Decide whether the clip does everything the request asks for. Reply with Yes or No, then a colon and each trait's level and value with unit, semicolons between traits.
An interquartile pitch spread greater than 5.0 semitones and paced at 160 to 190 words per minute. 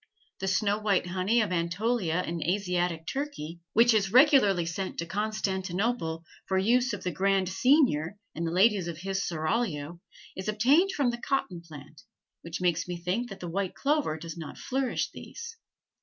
Yes: wide, 5.4 semitones; average, 170 wpm